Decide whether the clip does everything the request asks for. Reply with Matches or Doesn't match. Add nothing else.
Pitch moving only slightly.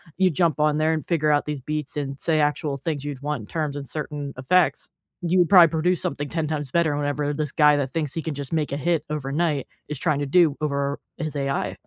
Matches